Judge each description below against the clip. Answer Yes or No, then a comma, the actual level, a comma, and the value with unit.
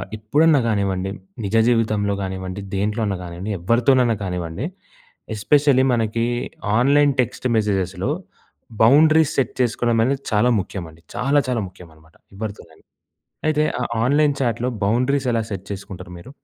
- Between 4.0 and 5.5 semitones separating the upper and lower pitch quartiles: Yes, average, 5.2 semitones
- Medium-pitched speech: No, low, 110 Hz